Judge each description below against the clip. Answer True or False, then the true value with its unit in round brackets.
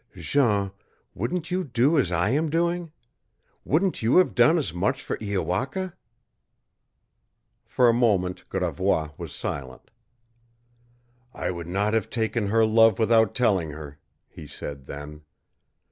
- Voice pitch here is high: False (110 Hz)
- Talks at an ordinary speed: False (130 wpm)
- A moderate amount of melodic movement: False (7.0 semitones)